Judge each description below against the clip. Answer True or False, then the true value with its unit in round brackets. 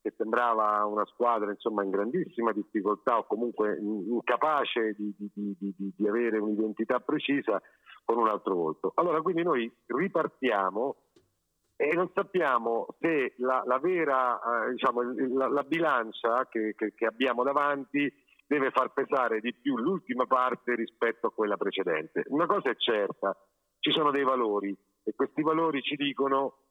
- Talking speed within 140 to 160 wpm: True (150 wpm)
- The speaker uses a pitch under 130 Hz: True (120 Hz)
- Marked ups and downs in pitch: False (4.9 semitones)